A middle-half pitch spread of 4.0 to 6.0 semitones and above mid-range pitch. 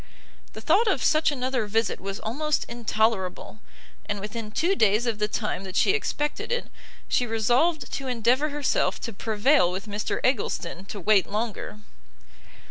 Yes: average, 4.7 semitones; high, 225 Hz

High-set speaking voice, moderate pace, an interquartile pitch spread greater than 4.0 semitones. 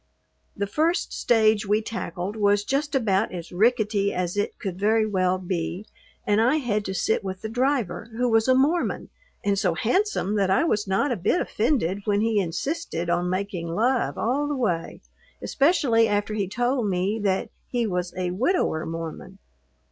Yes: high, 210 Hz; average, 175 wpm; average, 4.6 semitones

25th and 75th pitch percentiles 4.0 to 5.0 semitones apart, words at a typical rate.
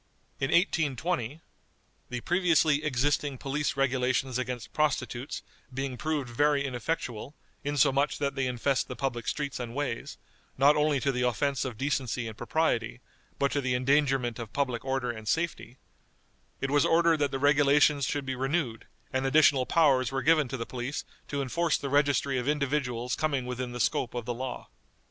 No: average, 2.7 semitones; average, 165 wpm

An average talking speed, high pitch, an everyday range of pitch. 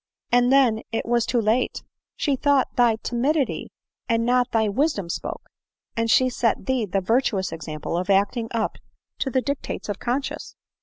Yes: average, 165 wpm; high, 235 Hz; average, 3.4 semitones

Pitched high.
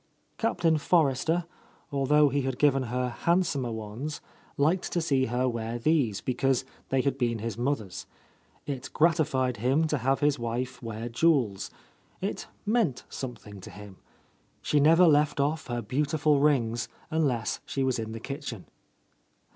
No: low, 135 Hz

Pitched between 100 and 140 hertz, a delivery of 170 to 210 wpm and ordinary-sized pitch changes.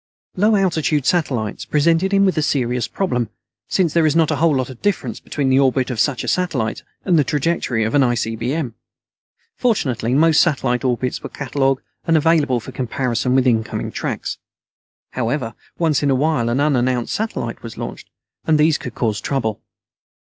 Yes: low, 135 Hz; average, 175 wpm; average, 4.7 semitones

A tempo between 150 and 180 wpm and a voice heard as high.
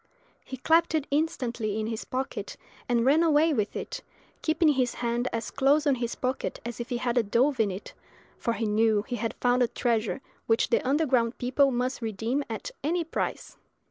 No: average, 195 wpm; high, 245 Hz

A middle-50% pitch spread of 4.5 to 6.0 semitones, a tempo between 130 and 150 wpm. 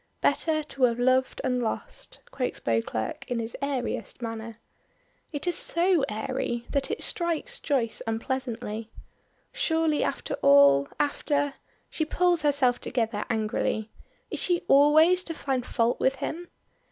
Yes: wide, 5.4 semitones; slow, 135 wpm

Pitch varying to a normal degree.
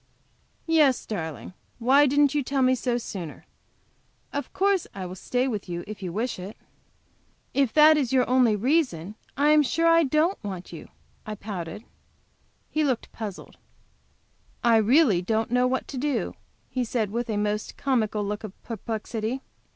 Yes: average, 4.9 semitones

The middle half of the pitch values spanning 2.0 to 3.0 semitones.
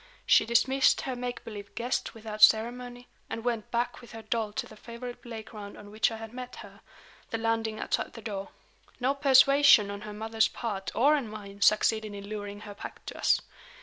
Yes: narrow, 2.5 semitones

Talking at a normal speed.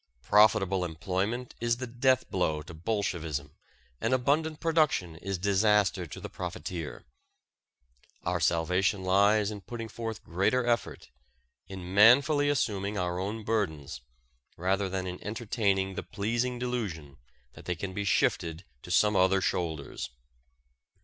No: slow, 130 wpm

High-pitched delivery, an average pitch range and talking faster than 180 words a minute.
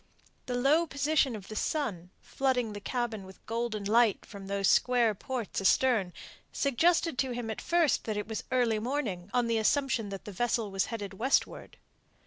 No: high, 230 Hz; average, 4.1 semitones; average, 175 wpm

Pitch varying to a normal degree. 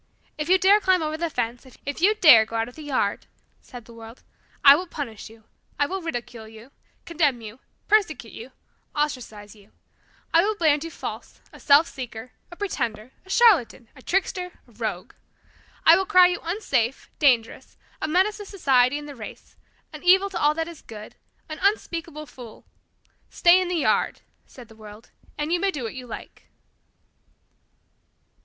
No: wide, 7.2 semitones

